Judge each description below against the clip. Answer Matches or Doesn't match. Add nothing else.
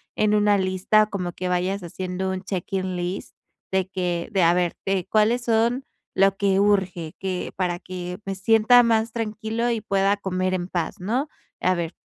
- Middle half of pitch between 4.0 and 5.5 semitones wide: Doesn't match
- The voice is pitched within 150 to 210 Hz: Matches